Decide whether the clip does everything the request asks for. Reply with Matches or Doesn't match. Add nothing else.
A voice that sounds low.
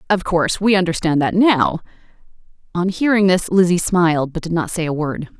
Doesn't match